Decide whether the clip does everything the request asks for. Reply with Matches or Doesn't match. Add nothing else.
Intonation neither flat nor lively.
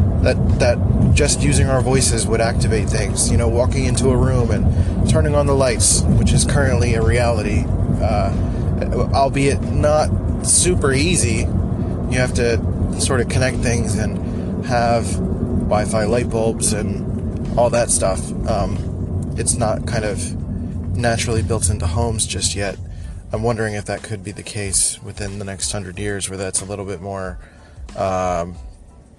Matches